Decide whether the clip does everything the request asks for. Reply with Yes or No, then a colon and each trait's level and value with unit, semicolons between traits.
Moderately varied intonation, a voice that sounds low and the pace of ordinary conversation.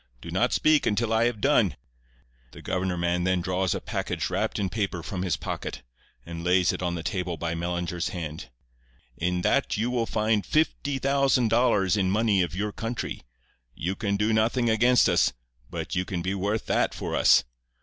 Yes: average, 4.2 semitones; very low, 95 Hz; average, 190 wpm